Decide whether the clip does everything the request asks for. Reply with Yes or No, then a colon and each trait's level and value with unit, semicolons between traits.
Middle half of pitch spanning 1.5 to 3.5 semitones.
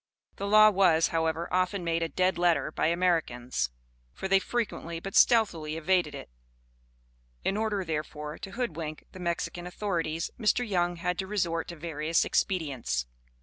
Yes: average, 3.1 semitones